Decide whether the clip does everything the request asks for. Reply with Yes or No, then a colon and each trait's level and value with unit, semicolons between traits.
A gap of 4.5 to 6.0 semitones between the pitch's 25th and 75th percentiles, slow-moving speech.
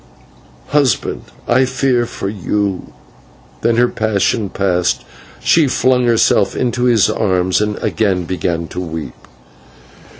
Yes: average, 5.0 semitones; slow, 125 wpm